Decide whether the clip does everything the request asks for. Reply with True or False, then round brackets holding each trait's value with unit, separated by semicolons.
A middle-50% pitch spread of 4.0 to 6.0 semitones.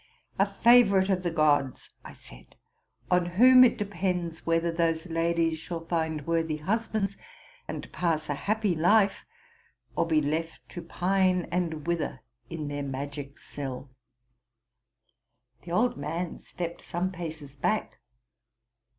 False (3.2 semitones)